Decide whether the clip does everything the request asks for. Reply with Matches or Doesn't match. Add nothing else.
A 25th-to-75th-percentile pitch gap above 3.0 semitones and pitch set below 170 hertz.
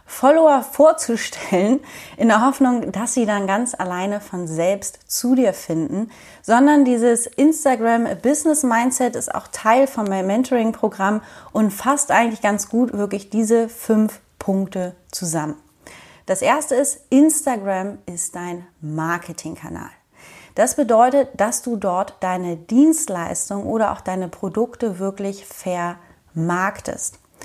Doesn't match